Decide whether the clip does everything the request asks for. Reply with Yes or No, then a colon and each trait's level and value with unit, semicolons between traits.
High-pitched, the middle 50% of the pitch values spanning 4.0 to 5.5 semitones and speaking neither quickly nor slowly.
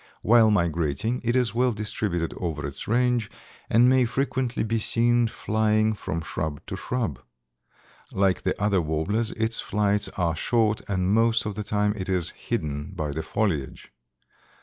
No: low, 105 Hz; average, 5.1 semitones; average, 155 wpm